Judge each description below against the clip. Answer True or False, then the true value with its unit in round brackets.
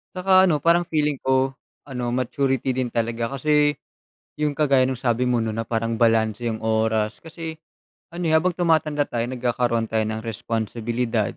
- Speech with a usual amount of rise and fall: True (4.6 semitones)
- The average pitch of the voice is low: True (125 Hz)